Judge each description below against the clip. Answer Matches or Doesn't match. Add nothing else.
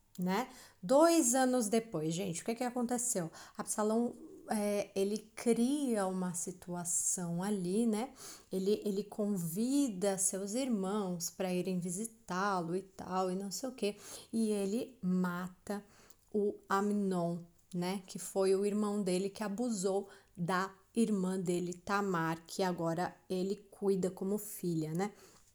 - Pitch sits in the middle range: Doesn't match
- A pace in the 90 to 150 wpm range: Matches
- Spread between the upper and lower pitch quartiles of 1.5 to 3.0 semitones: Matches